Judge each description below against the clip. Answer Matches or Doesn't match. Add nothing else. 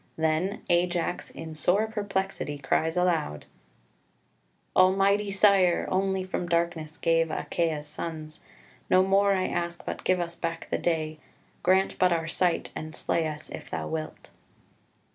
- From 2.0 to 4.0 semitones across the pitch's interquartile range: Matches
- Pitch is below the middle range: Doesn't match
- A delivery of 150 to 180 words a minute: Doesn't match